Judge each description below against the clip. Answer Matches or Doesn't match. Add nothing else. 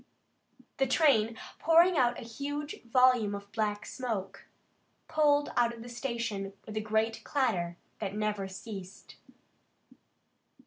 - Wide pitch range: Doesn't match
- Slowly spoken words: Matches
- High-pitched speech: Matches